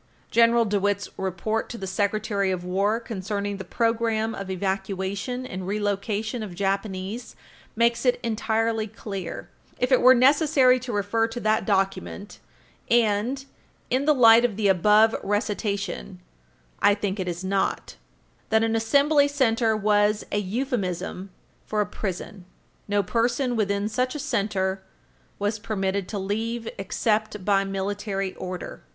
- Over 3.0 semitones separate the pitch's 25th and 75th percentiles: No, average, 2.7 semitones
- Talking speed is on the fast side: No, average, 140 wpm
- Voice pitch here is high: Yes, high, 210 Hz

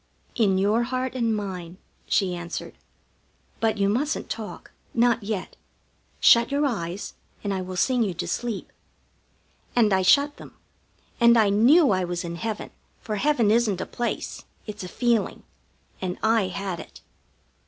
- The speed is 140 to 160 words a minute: Yes, average, 155 wpm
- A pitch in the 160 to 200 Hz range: No, high, 215 Hz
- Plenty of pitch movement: No, average, 4.0 semitones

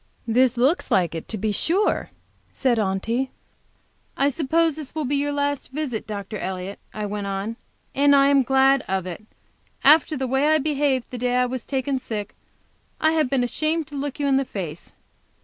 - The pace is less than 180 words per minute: No, average, 190 wpm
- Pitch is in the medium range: No, very high, 265 Hz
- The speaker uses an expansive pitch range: No, average, 4.9 semitones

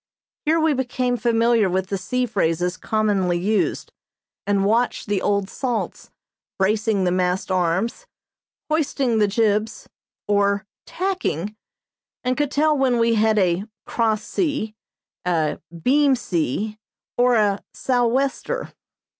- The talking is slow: Yes, slow, 125 wpm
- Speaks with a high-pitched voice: Yes, high, 220 Hz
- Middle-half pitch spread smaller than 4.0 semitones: No, average, 4.3 semitones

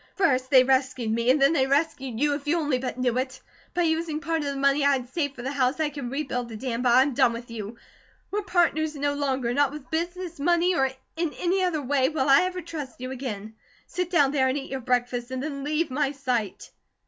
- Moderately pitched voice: No, very high, 275 Hz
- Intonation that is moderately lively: Yes, average, 3.5 semitones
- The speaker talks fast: Yes, fast, 240 wpm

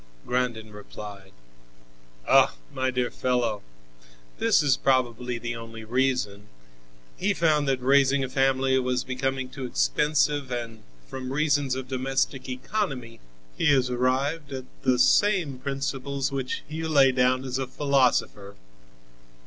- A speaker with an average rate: No, slow, 130 wpm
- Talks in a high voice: No, low, 130 Hz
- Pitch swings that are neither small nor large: No, narrow, 1.8 semitones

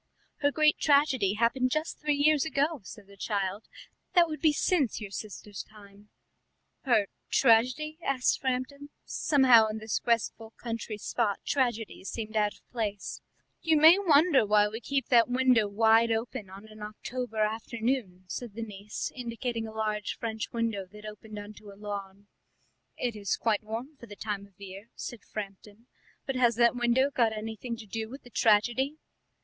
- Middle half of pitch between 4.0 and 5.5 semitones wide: No, average, 3.5 semitones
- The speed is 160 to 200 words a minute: Yes, average, 170 wpm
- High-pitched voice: Yes, high, 225 Hz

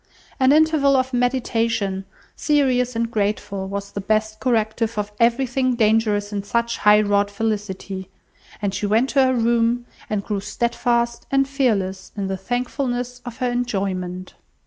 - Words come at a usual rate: Yes, average, 145 wpm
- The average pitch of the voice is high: Yes, high, 225 Hz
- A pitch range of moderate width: Yes, average, 3.4 semitones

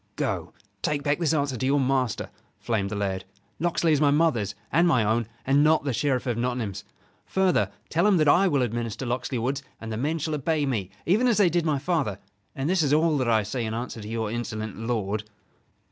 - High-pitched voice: No, low, 135 Hz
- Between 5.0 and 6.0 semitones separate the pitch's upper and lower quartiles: Yes, wide, 5.6 semitones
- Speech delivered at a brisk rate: Yes, fast, 220 wpm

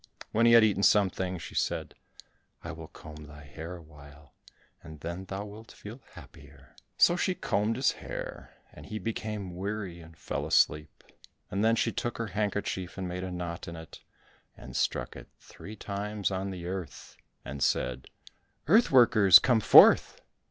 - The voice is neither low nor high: No, very low, 95 Hz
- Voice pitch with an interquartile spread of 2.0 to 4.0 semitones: No, average, 4.6 semitones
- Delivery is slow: No, average, 170 wpm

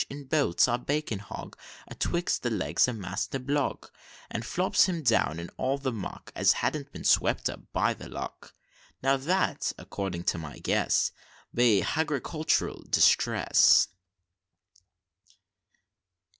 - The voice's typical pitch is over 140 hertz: No, low, 130 Hz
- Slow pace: Yes, slow, 130 wpm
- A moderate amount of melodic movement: No, wide, 6.2 semitones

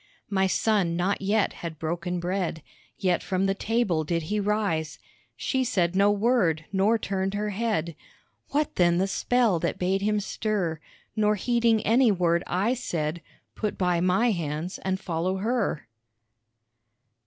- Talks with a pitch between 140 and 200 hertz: Yes, high, 190 Hz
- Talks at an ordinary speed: Yes, average, 150 wpm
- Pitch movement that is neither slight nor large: Yes, average, 3.7 semitones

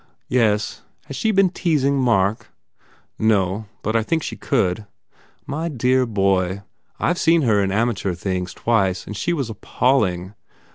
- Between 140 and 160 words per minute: Yes, average, 155 wpm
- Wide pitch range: Yes, wide, 5.8 semitones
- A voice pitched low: Yes, low, 110 Hz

